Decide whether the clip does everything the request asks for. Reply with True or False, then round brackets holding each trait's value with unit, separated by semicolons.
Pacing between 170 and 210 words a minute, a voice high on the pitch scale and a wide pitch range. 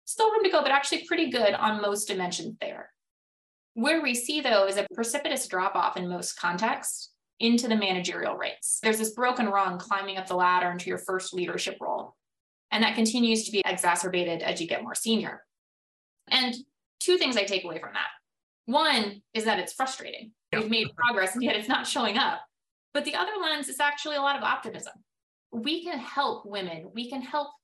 True (200 wpm; 225 Hz; 6.6 semitones)